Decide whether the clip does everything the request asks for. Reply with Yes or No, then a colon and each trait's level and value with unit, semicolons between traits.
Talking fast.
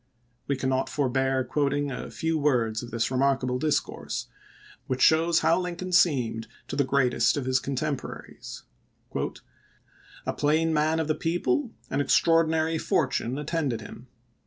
No: slow, 135 wpm